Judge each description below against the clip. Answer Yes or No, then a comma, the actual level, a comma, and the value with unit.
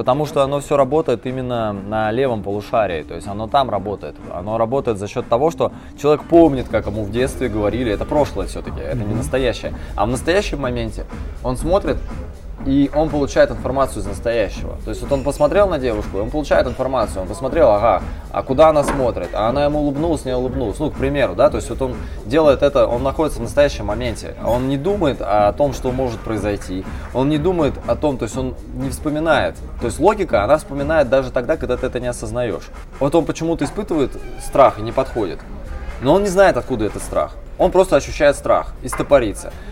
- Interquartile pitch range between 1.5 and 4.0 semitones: No, average, 5.1 semitones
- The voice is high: No, low, 130 Hz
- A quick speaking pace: Yes, fast, 200 wpm